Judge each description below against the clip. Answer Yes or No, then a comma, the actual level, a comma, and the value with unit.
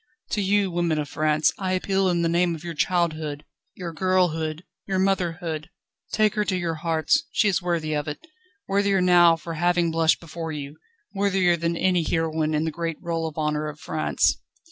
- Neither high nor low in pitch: Yes, medium, 170 Hz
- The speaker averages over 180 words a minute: Yes, average, 190 wpm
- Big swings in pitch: No, average, 2.7 semitones